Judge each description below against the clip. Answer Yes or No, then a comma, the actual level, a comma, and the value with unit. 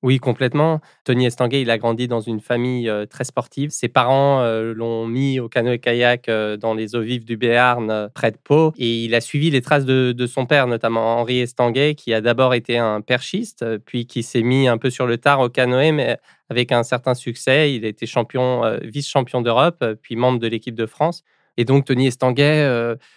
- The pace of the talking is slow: No, average, 210 wpm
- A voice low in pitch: Yes, low, 125 Hz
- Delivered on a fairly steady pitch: Yes, narrow, 2.3 semitones